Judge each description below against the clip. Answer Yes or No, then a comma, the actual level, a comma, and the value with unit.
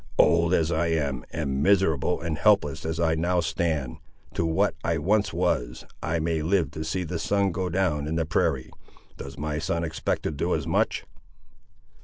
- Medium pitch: No, very low, 80 Hz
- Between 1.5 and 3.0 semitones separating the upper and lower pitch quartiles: Yes, narrow, 2.5 semitones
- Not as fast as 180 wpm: No, average, 185 wpm